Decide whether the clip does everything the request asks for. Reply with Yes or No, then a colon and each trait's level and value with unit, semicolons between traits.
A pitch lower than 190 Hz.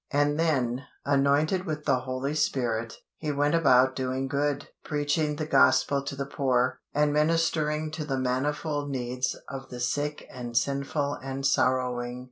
Yes: medium, 140 Hz